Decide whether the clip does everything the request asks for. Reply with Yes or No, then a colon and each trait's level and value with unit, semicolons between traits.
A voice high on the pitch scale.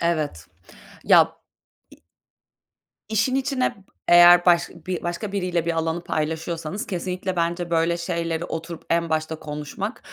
No: medium, 170 Hz